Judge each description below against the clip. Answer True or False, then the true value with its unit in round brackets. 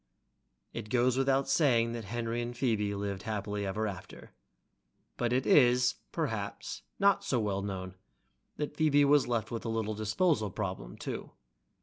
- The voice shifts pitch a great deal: False (3.8 semitones)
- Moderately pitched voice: False (115 Hz)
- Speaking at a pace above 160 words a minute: False (155 wpm)